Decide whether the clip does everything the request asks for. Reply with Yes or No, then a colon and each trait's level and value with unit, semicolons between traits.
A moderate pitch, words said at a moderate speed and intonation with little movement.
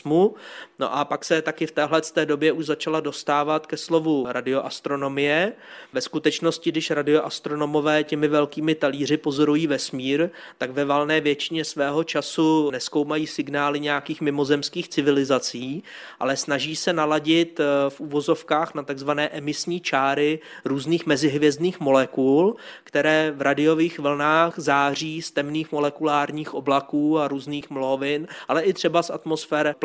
Yes: medium, 150 Hz; average, 130 wpm; narrow, 1.7 semitones